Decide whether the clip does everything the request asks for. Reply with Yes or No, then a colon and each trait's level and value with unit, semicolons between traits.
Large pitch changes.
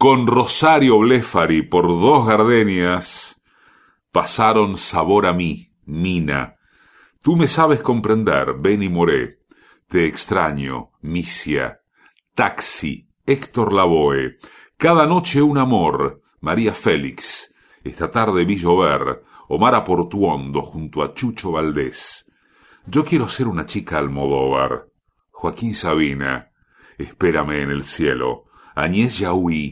Yes: wide, 6.9 semitones